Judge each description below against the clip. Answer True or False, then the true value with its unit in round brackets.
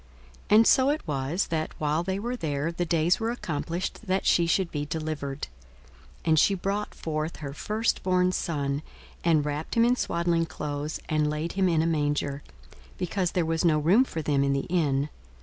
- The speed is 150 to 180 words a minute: False (190 wpm)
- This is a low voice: False (165 Hz)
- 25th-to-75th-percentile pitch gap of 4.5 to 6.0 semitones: False (3.7 semitones)